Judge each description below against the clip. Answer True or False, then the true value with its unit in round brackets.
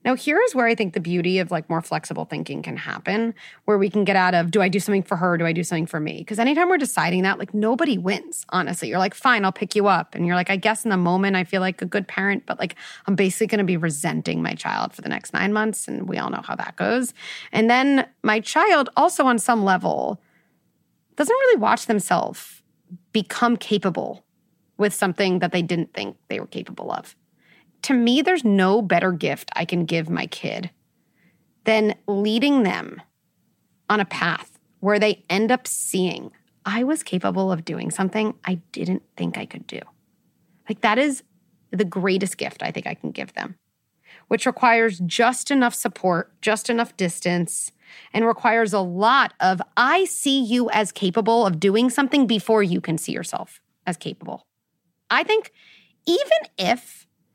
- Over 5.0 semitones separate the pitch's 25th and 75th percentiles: False (4.4 semitones)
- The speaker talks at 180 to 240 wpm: True (195 wpm)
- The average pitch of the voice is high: True (205 Hz)